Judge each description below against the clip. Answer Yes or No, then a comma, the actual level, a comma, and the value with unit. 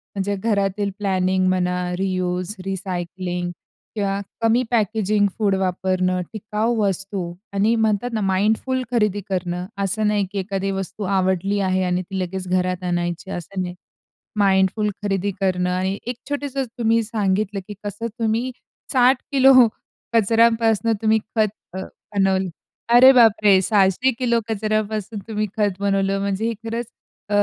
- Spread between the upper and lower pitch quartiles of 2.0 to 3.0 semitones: Yes, average, 2.7 semitones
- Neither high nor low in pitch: No, high, 200 Hz